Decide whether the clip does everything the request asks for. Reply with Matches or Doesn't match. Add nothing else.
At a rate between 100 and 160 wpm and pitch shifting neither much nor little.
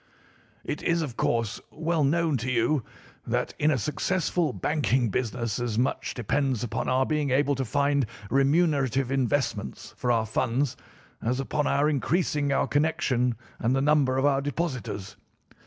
Matches